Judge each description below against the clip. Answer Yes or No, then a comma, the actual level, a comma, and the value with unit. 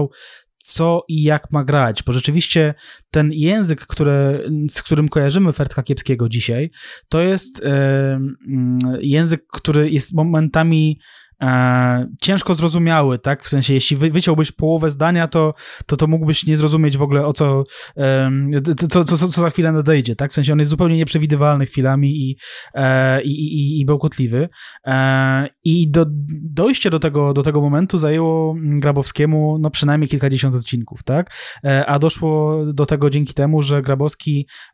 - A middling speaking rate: Yes, average, 150 wpm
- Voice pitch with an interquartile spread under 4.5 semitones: Yes, narrow, 2.5 semitones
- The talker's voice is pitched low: No, medium, 150 Hz